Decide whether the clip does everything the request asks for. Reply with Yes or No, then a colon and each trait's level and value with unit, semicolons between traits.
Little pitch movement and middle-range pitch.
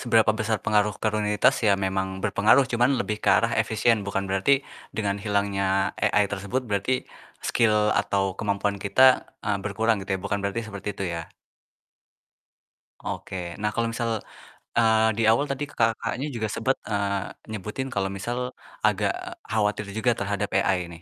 No: narrow, 2.3 semitones; low, 105 Hz